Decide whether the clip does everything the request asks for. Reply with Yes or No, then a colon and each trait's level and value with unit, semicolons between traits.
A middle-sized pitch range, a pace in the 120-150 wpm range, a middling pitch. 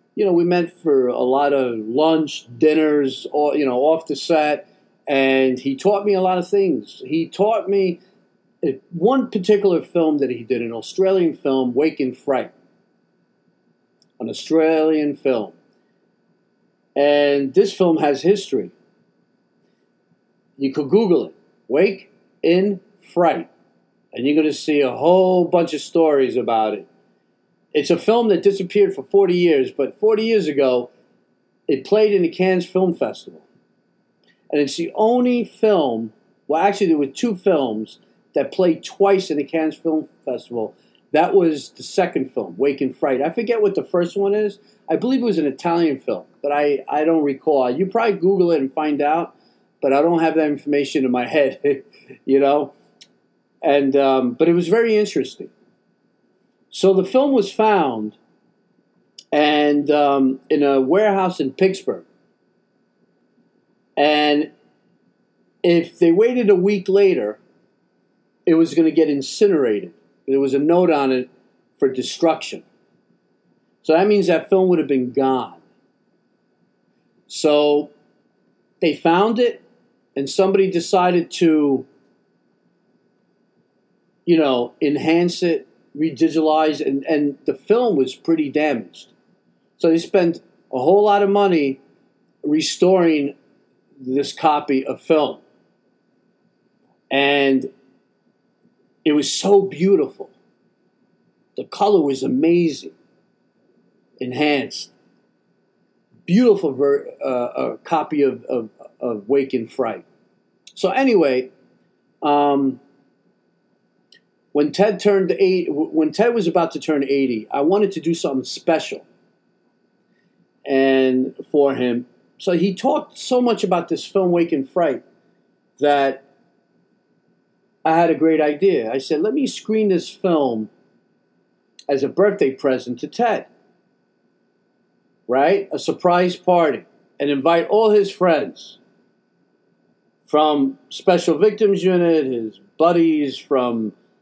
No: wide, 5.7 semitones; slow, 135 wpm; medium, 160 Hz